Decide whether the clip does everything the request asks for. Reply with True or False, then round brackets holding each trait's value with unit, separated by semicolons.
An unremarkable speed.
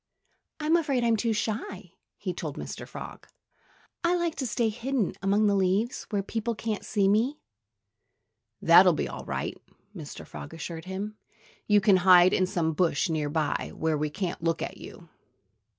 True (165 wpm)